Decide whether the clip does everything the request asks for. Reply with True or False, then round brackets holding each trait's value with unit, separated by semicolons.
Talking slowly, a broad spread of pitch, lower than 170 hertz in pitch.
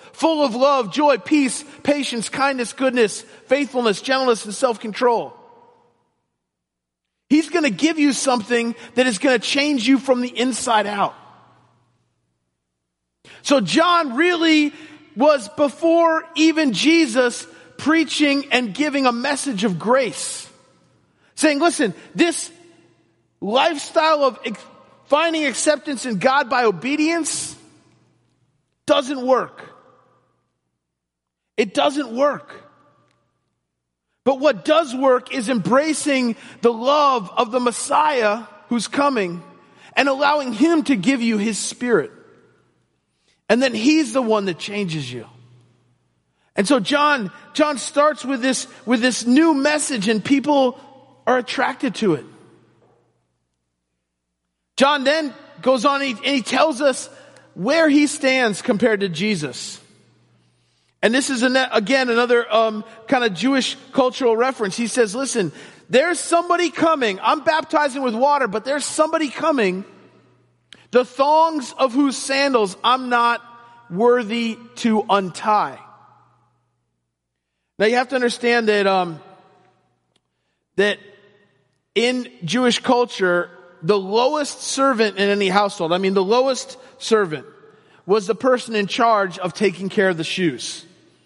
False (125 wpm; 5.8 semitones; 250 Hz)